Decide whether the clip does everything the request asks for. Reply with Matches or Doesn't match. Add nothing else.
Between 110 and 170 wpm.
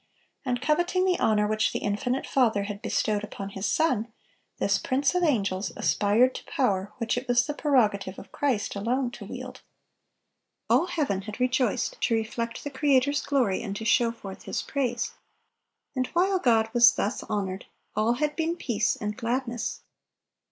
Matches